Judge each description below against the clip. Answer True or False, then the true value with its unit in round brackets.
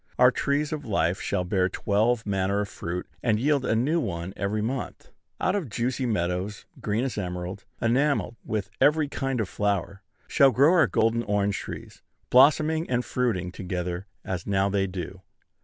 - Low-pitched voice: True (105 Hz)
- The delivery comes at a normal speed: True (170 wpm)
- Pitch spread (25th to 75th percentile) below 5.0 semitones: False (5.4 semitones)